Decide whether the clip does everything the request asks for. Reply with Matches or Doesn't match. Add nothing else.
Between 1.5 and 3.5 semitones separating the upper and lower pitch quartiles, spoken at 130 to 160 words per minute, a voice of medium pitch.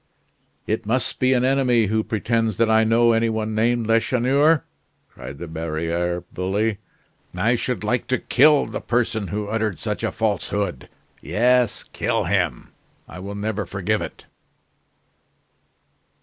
Doesn't match